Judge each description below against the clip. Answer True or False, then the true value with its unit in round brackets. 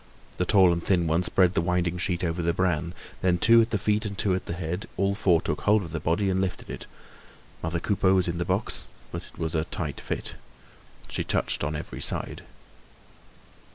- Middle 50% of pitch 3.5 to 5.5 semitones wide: False (2.4 semitones)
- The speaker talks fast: True (215 wpm)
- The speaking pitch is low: True (90 Hz)